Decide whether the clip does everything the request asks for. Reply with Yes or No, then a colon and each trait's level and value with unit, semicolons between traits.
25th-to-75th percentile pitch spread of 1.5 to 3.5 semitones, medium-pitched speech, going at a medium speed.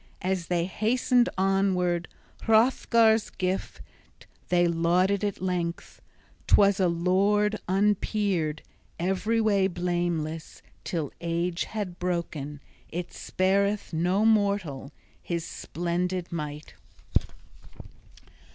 No: average, 2.9 semitones; medium, 180 Hz; slow, 90 wpm